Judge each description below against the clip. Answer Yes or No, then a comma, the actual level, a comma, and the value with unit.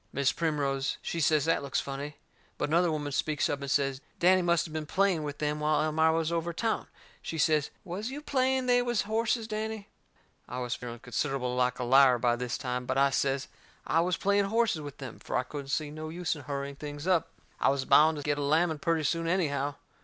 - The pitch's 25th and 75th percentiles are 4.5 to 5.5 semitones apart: No, average, 3.8 semitones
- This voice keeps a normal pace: No, fast, 220 wpm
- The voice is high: No, medium, 150 Hz